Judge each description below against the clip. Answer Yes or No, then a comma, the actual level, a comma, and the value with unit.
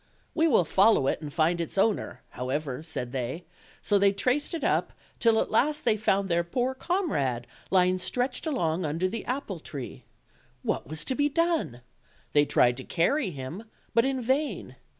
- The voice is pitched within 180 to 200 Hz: Yes, high, 190 Hz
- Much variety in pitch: Yes, wide, 9.0 semitones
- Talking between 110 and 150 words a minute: No, average, 175 wpm